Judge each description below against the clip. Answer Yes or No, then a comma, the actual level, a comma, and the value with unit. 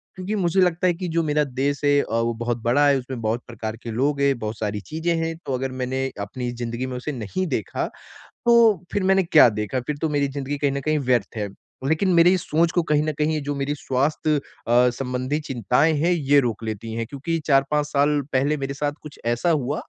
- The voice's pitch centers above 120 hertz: Yes, medium, 140 Hz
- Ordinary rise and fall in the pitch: Yes, average, 3.8 semitones